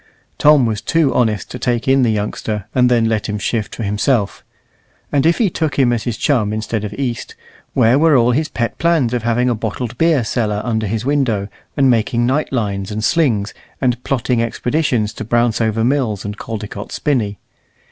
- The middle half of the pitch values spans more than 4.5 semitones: No, average, 3.7 semitones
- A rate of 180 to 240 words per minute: Yes, average, 190 wpm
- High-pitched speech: No, low, 120 Hz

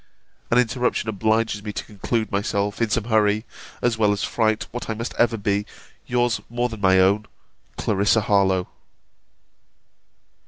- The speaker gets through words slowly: No, average, 150 wpm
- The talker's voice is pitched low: Yes, low, 110 Hz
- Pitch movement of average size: No, narrow, 2.2 semitones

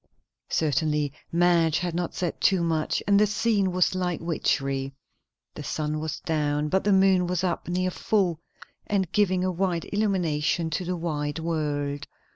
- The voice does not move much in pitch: No, average, 3.3 semitones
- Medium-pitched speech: Yes, medium, 170 Hz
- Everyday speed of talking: Yes, average, 160 wpm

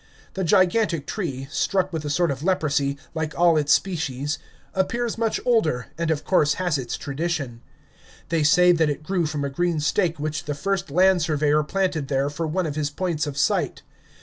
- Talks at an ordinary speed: Yes, average, 190 wpm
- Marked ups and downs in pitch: No, average, 3.6 semitones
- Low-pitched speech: No, medium, 160 Hz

